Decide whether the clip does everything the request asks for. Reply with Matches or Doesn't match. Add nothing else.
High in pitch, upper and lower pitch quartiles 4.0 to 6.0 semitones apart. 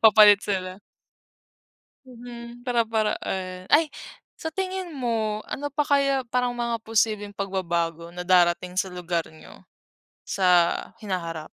Matches